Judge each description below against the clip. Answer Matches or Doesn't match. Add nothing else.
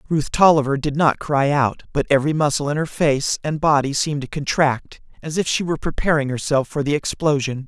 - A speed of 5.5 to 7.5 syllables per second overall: Matches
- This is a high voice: Doesn't match